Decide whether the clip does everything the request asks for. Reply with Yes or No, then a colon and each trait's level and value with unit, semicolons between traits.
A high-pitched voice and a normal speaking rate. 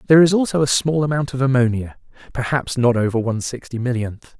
No: low, 130 Hz; average, 190 wpm